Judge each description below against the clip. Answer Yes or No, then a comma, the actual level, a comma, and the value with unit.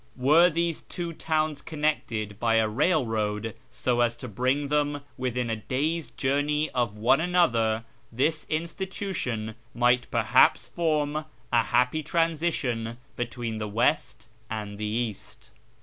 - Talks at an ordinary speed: No, slow, 130 wpm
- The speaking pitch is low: Yes, low, 125 Hz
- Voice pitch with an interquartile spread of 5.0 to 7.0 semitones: Yes, wide, 5.4 semitones